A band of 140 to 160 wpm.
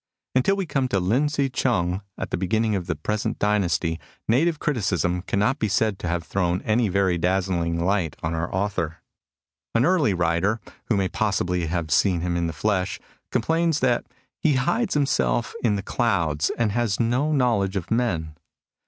No: average, 180 wpm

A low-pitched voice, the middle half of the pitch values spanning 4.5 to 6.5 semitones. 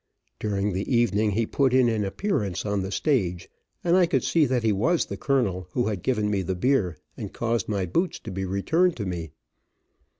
Yes: low, 110 Hz; wide, 5.4 semitones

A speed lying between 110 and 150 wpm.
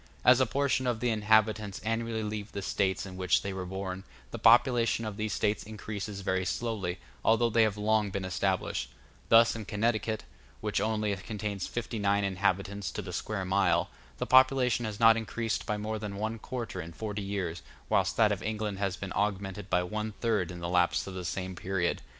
No: average, 195 wpm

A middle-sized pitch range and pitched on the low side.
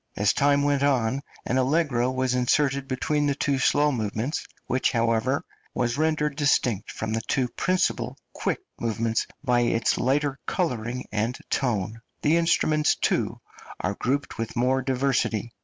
Yes: average, 3.5 semitones; low, 130 Hz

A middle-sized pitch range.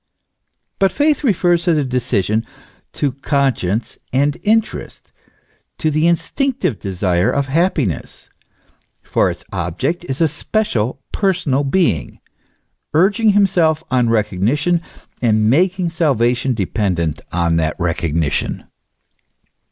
No: wide, 8.5 semitones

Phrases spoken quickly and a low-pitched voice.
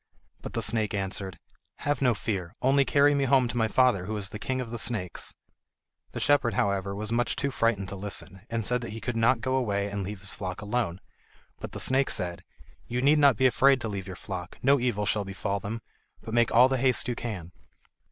Yes: fast, 225 wpm; low, 115 Hz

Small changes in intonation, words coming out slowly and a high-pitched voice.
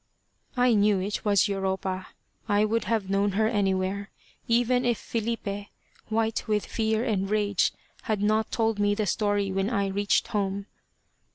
No: narrow, 2.0 semitones; average, 155 wpm; high, 205 Hz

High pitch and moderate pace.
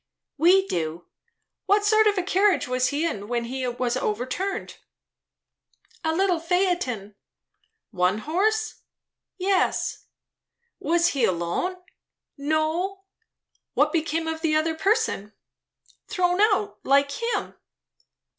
No: very high, 325 Hz; slow, 110 wpm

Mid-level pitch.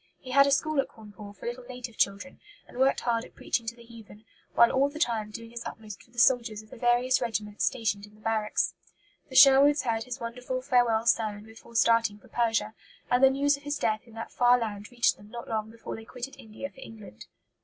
No: high, 230 Hz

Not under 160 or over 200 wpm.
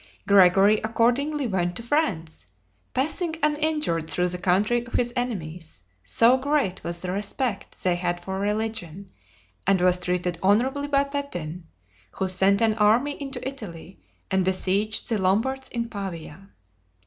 No: average, 140 wpm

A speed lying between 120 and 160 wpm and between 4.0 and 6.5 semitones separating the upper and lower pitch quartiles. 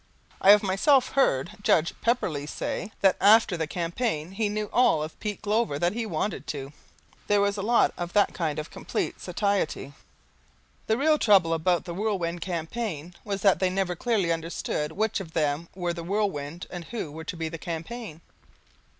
No: average, 180 wpm; average, 4.4 semitones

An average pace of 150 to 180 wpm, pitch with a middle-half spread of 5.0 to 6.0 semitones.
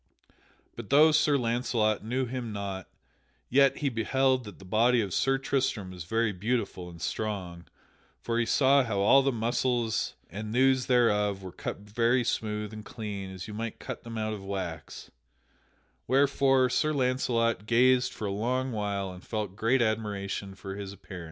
No: average, 170 wpm; average, 4.1 semitones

